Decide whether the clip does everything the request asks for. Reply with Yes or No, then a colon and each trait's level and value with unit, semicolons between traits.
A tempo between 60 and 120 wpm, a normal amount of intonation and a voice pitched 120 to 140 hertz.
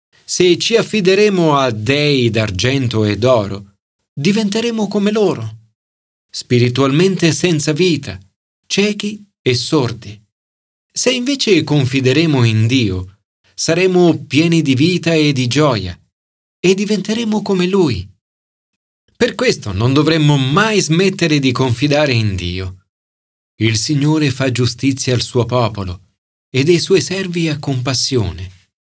No: slow, 115 wpm; wide, 8.4 semitones; low, 135 Hz